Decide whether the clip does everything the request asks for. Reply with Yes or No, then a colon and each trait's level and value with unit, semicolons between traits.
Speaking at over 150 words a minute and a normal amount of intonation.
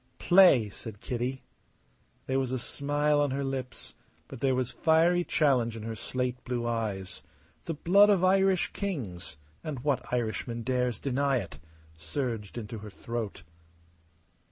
No: average, 145 wpm; average, 4.2 semitones